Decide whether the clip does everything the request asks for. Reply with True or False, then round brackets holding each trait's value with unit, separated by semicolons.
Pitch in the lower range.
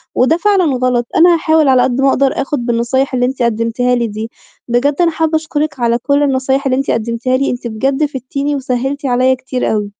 False (260 Hz)